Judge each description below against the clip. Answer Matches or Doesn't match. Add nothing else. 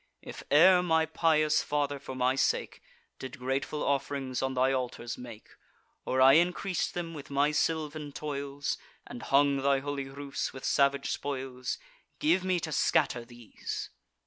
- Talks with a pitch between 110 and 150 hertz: Matches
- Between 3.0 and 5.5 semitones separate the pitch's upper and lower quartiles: Doesn't match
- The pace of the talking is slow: Doesn't match